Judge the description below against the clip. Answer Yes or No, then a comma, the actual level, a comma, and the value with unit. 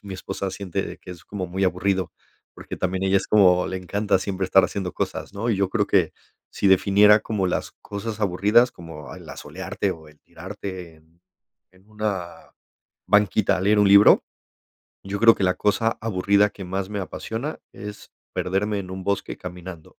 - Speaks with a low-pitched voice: Yes, very low, 95 Hz